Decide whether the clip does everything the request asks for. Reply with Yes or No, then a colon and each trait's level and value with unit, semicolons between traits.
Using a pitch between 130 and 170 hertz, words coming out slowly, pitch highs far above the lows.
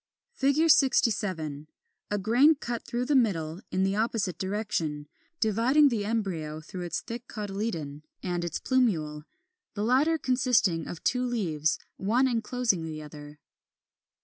No: high, 205 Hz; slow, 130 wpm; wide, 7.0 semitones